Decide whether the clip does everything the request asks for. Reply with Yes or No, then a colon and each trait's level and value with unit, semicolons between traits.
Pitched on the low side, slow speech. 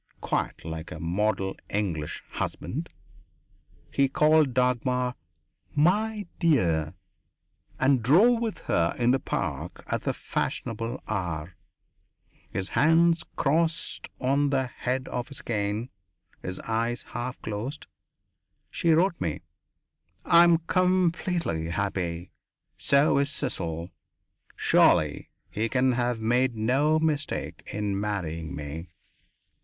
Yes: low, 125 Hz; slow, 110 wpm